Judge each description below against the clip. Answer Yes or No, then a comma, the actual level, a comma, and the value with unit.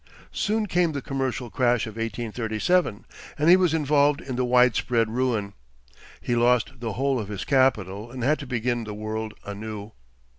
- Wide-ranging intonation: No, average, 3.7 semitones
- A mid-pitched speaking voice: No, low, 120 Hz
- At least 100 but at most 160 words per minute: No, average, 170 wpm